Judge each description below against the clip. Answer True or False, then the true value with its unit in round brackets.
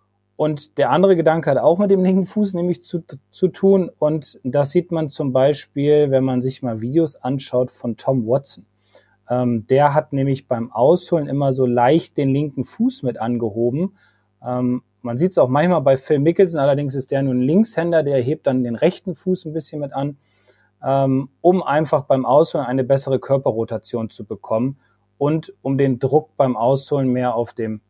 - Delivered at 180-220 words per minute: True (185 wpm)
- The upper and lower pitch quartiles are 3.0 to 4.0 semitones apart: False (4.4 semitones)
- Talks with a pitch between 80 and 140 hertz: True (135 Hz)